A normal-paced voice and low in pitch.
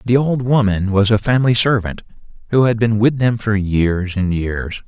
Yes: average, 195 wpm; low, 110 Hz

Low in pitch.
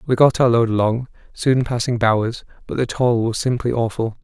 Yes: low, 120 Hz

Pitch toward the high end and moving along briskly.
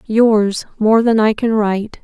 No: high, 215 Hz; average, 175 wpm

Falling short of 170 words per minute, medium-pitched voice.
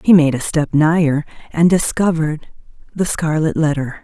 Yes: average, 150 wpm; medium, 155 Hz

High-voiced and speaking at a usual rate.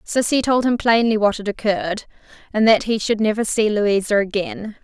Yes: high, 215 Hz; average, 185 wpm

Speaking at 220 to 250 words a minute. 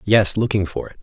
Yes: fast, 235 wpm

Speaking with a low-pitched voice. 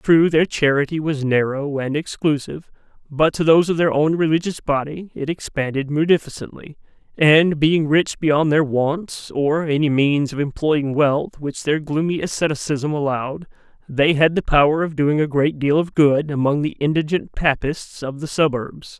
No: medium, 150 Hz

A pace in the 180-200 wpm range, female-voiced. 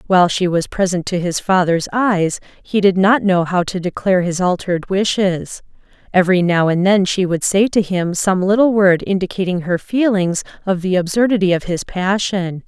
Yes: average, 185 wpm; female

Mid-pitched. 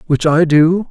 Yes: medium, 160 Hz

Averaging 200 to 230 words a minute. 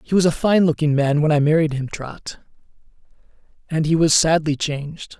No: average, 175 wpm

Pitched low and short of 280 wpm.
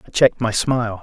Yes: low, 115 Hz; fast, 235 wpm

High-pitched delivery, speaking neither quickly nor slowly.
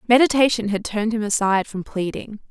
Yes: high, 215 Hz; average, 170 wpm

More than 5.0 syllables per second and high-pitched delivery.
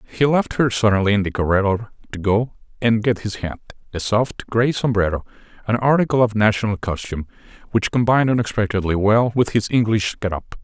No: 5.7 syllables/s; low, 110 Hz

